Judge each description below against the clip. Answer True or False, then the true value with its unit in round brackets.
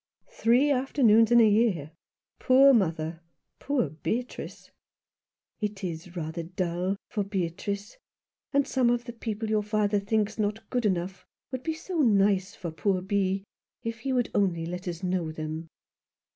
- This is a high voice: True (205 Hz)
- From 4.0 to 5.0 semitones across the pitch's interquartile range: True (4.6 semitones)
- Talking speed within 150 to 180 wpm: True (160 wpm)